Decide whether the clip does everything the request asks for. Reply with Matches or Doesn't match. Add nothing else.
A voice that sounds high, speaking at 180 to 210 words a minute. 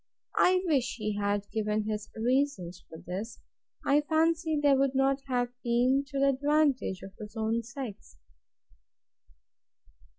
Doesn't match